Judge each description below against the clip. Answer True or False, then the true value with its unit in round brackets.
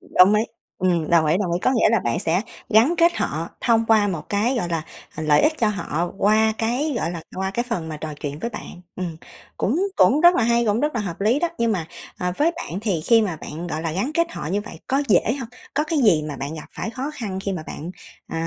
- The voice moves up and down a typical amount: False (5.9 semitones)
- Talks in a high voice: True (200 Hz)